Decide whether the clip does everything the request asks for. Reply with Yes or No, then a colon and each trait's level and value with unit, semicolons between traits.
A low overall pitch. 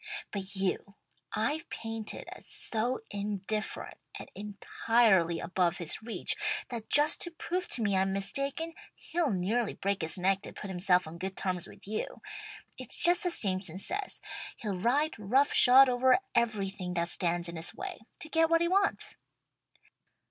No: high, 210 Hz